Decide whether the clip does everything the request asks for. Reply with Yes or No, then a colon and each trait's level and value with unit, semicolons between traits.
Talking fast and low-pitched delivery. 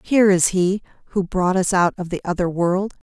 No: fast, 215 wpm; medium, 185 Hz